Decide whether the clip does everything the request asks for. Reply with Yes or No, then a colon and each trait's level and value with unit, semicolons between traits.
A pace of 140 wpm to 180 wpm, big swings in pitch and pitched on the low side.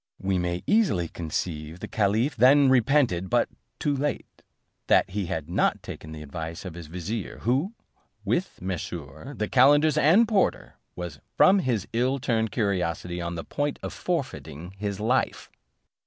Yes: average, 155 wpm; wide, 7.8 semitones; low, 105 Hz